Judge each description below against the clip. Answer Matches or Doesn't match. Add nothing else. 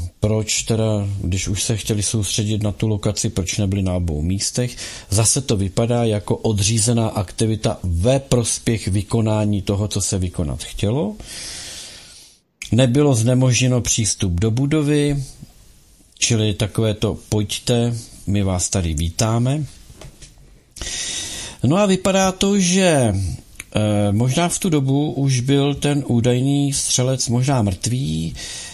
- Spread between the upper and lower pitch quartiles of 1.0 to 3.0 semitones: Doesn't match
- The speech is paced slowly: Doesn't match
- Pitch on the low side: Matches